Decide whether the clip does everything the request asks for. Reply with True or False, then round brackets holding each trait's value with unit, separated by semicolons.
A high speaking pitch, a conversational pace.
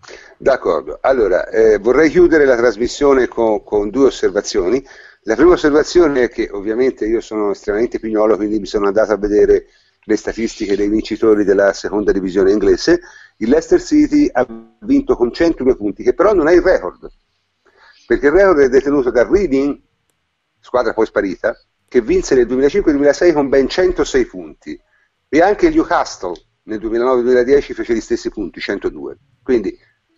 True (345 Hz; 155 wpm)